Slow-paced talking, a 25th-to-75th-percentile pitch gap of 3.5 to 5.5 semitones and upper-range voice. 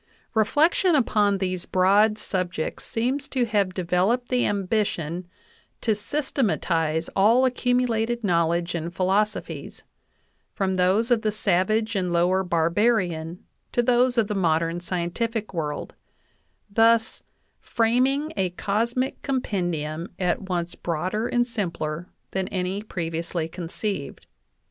Yes: slow, 115 wpm; average, 4.7 semitones; high, 195 Hz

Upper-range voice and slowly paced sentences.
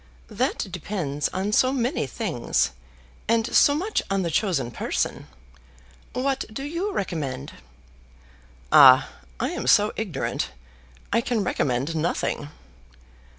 Yes: high, 200 Hz; slow, 115 wpm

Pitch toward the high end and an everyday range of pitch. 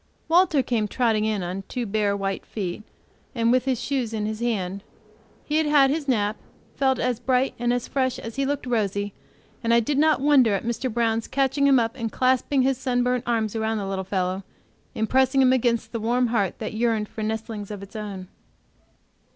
Yes: high, 235 Hz; average, 3.4 semitones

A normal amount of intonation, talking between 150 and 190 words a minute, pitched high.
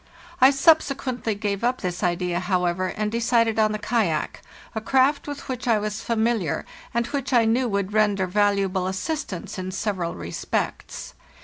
Yes: average, 4.2 semitones; average, 170 wpm; high, 215 Hz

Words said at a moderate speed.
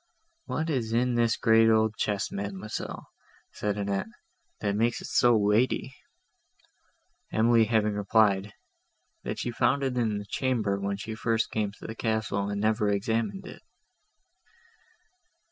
Yes: average, 145 wpm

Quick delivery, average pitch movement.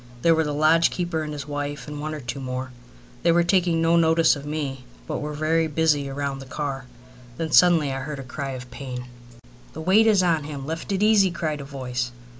Yes: fast, 225 wpm; average, 3.1 semitones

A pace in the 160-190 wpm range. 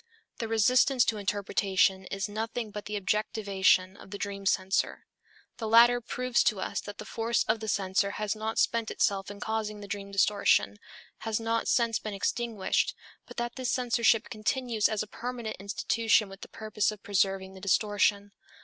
Yes: average, 175 wpm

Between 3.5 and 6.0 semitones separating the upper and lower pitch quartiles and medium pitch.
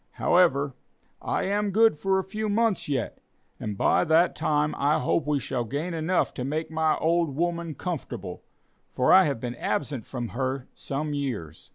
Yes: average, 4.5 semitones; medium, 150 Hz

